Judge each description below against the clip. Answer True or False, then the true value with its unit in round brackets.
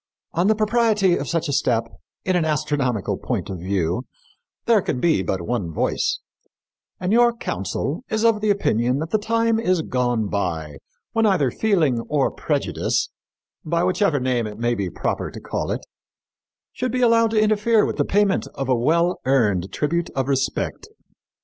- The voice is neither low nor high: True (155 Hz)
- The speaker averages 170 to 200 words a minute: True (175 wpm)